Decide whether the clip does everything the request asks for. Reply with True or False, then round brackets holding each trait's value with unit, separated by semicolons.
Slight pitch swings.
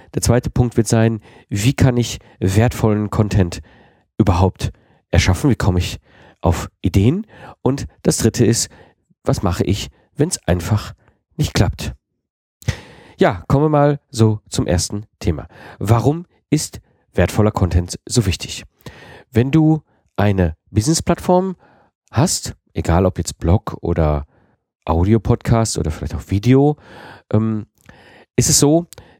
False (5.1 semitones)